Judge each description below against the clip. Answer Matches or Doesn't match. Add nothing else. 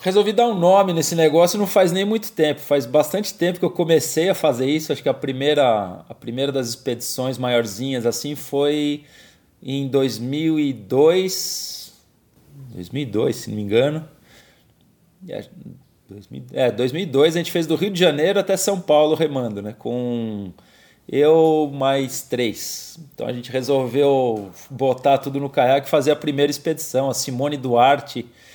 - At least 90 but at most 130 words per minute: Doesn't match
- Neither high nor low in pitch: Matches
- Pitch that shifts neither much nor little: Matches